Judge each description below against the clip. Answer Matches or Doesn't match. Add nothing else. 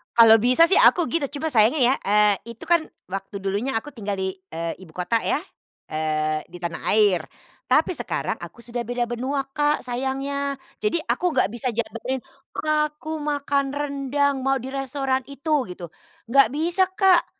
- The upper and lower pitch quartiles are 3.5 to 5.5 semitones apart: Matches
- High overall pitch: Matches